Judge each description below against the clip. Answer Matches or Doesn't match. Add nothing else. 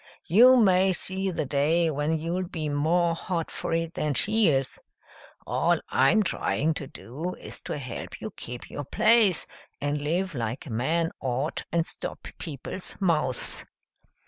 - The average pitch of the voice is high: Doesn't match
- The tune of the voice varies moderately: Matches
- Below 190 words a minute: Matches